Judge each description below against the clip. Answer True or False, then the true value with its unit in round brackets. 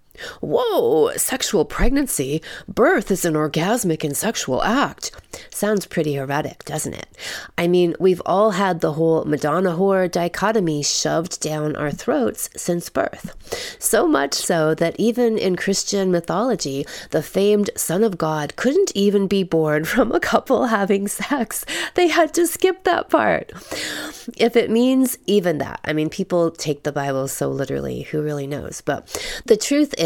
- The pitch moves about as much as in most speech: False (7.2 semitones)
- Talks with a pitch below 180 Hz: False (190 Hz)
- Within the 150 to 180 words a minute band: True (160 wpm)